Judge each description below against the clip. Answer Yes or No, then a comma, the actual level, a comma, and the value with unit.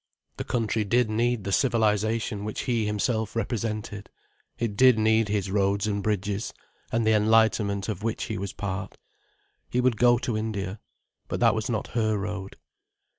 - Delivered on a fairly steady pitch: Yes, narrow, 2.0 semitones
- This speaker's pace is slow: No, average, 165 wpm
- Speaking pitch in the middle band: No, low, 110 Hz